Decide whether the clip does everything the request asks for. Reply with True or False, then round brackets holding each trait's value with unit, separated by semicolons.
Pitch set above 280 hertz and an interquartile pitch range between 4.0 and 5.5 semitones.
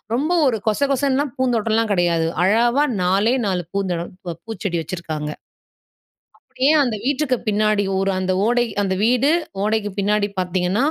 False (215 Hz; 4.7 semitones)